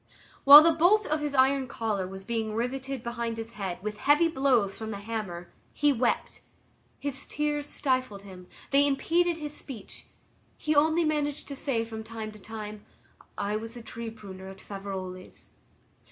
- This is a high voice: Yes, high, 235 Hz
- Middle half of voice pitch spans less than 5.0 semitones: No, wide, 5.4 semitones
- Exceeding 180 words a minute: No, average, 170 wpm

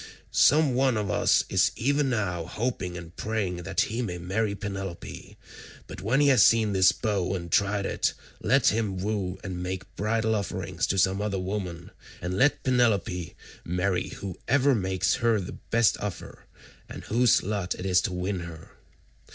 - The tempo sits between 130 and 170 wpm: Yes, average, 165 wpm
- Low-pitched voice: Yes, low, 100 Hz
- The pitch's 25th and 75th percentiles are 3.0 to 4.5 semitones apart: Yes, average, 3.7 semitones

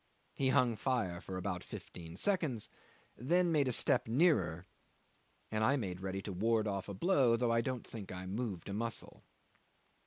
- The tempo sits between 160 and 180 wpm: Yes, average, 175 wpm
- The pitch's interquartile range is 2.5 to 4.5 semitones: No, average, 5.3 semitones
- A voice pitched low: Yes, low, 110 Hz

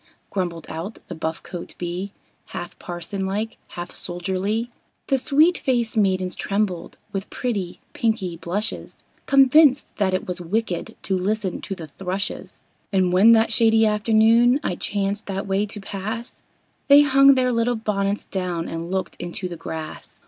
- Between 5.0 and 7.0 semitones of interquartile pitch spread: No, average, 3.8 semitones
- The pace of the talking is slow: No, average, 155 wpm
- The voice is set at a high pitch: Yes, high, 200 Hz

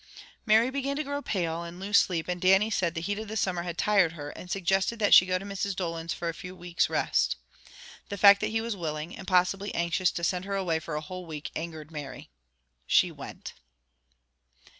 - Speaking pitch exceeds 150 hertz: Yes, medium, 185 Hz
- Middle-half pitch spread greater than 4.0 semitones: No, average, 3.1 semitones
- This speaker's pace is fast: Yes, fast, 210 wpm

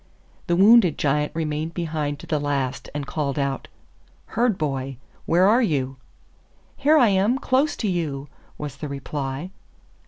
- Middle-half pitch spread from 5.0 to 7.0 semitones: Yes, wide, 5.5 semitones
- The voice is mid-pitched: Yes, medium, 155 Hz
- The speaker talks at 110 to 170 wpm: Yes, average, 150 wpm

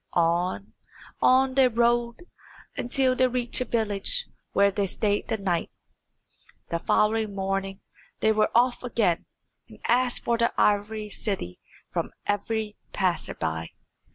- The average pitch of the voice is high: Yes, high, 215 Hz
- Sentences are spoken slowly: Yes, slow, 125 wpm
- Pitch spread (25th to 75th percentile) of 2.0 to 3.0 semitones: No, average, 3.6 semitones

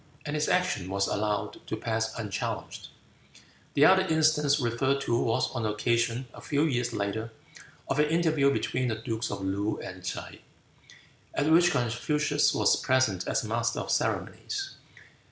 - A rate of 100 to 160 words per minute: Yes, average, 155 wpm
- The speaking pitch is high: No, low, 120 Hz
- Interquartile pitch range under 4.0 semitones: No, average, 5.1 semitones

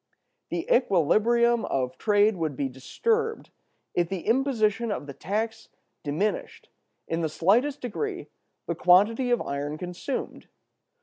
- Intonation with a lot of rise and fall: Yes, wide, 6.4 semitones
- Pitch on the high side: Yes, high, 210 Hz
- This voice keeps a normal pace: No, slow, 125 wpm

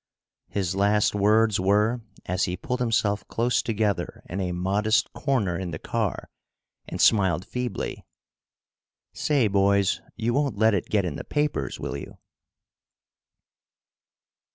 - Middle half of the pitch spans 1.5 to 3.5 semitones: Yes, average, 3.1 semitones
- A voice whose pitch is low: Yes, low, 105 Hz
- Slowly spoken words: Yes, slow, 130 wpm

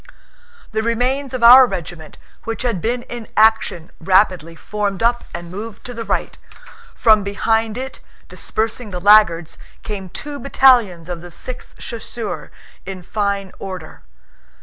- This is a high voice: Yes, high, 215 Hz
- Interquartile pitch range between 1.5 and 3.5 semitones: No, average, 4.3 semitones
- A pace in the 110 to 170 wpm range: Yes, average, 140 wpm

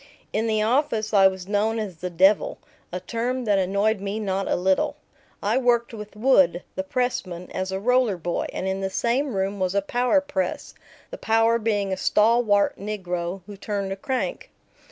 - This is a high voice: Yes, high, 205 Hz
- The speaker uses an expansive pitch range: No, average, 3.5 semitones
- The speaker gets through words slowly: No, average, 185 wpm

